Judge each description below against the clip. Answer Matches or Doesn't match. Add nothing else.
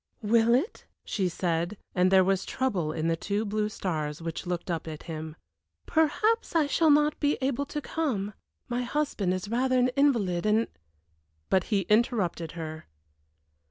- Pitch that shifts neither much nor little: Doesn't match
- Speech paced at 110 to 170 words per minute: Matches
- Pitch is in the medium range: Doesn't match